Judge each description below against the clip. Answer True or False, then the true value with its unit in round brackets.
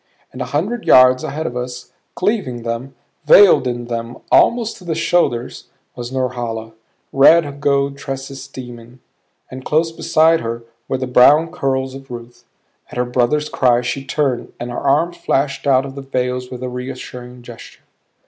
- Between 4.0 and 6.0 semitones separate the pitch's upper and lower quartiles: False (2.8 semitones)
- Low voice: True (130 Hz)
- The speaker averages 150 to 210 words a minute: True (160 wpm)